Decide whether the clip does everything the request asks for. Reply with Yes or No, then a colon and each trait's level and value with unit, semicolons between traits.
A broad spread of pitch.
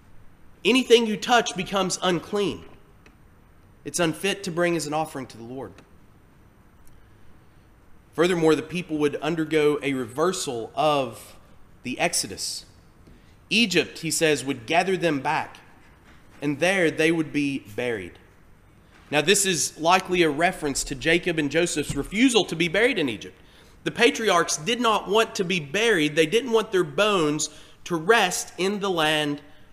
Yes: wide, 6.4 semitones